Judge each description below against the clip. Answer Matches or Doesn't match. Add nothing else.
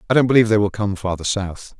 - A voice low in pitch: Matches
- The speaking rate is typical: Doesn't match